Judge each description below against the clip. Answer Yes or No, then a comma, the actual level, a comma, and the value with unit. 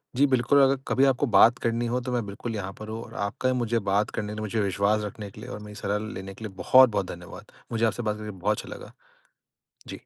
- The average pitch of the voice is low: Yes, low, 110 Hz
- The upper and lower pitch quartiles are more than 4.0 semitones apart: No, average, 2.9 semitones